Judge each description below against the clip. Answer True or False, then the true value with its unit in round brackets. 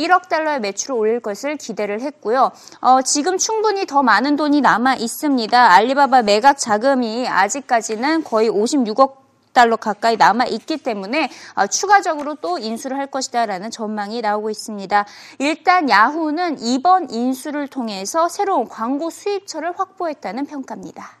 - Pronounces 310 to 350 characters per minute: True (340 characters per minute)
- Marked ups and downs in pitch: True (5.7 semitones)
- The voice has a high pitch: True (270 Hz)